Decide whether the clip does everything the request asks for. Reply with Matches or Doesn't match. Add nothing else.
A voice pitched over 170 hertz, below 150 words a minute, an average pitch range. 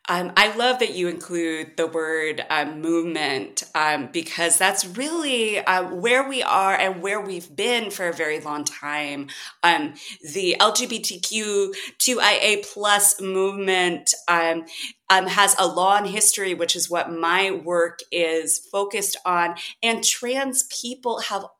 Matches